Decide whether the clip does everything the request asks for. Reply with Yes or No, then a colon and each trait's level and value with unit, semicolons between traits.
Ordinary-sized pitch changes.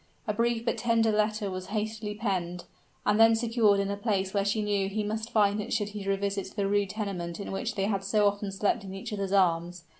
No: narrow, 1.8 semitones